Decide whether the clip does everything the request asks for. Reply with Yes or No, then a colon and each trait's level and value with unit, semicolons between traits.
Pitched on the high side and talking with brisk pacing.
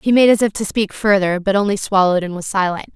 Yes: high, 200 Hz; fast, 265 wpm